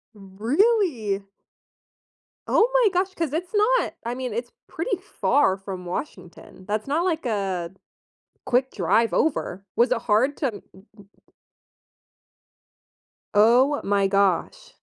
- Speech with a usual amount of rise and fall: No, wide, 8.8 semitones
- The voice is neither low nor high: No, high, 240 Hz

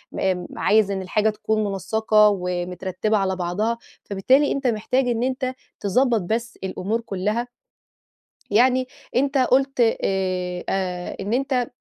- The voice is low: No, high, 215 Hz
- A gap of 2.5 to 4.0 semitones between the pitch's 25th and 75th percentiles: No, average, 4.6 semitones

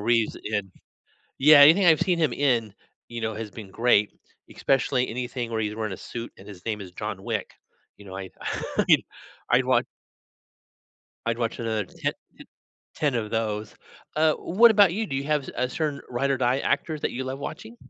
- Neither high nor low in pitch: No, low, 120 Hz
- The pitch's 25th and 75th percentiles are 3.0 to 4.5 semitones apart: No, average, 5.0 semitones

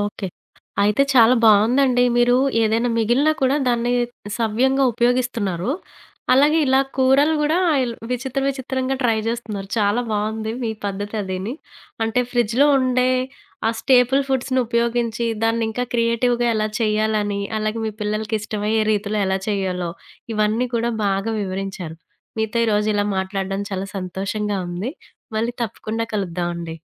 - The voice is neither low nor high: No, high, 225 Hz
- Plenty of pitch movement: No, average, 3.3 semitones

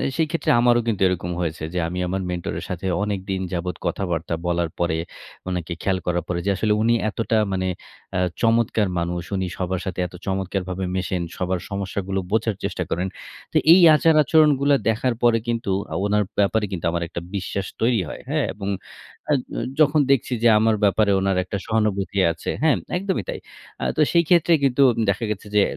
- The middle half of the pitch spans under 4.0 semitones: No, average, 4.3 semitones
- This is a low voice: Yes, low, 100 Hz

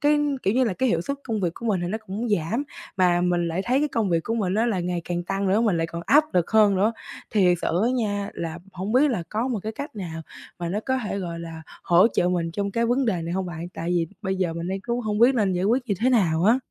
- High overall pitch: Yes, high, 195 Hz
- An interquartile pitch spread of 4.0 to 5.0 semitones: Yes, average, 4.7 semitones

